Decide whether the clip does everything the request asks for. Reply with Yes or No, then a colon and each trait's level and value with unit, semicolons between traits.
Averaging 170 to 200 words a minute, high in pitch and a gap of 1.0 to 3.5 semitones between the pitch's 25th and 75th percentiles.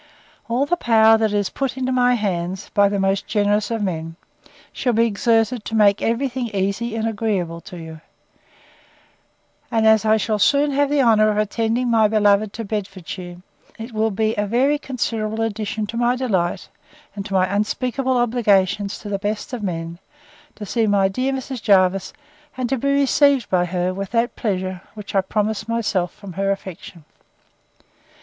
Yes: average, 175 wpm; high, 215 Hz; average, 3.2 semitones